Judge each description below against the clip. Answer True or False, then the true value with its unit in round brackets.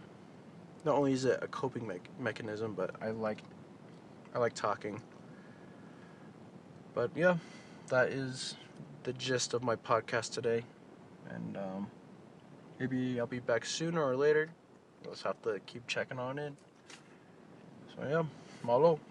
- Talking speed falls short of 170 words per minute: True (140 wpm)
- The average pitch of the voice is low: True (130 Hz)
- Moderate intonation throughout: False (5.7 semitones)